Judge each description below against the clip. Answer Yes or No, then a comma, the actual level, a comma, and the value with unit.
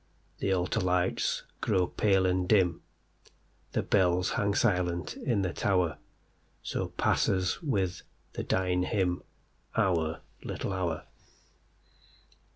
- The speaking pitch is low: Yes, very low, 90 Hz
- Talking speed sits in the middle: No, slow, 95 wpm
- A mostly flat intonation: Yes, narrow, 1.5 semitones